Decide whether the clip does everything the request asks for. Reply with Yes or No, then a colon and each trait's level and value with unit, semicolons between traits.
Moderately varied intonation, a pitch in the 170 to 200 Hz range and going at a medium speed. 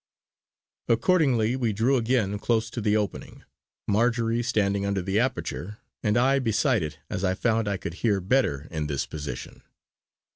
No: average, 3.4 semitones; low, 110 Hz; average, 155 wpm